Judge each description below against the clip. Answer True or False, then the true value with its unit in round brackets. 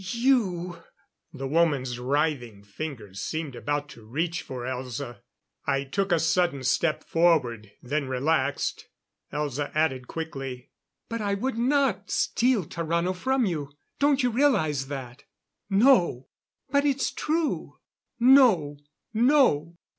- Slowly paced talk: True (125 wpm)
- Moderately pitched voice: True (160 Hz)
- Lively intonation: True (8.0 semitones)